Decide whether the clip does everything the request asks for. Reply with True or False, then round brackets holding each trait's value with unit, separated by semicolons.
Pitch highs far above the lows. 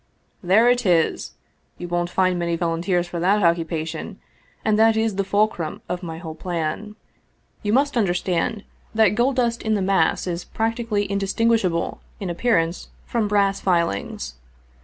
False (4.2 semitones)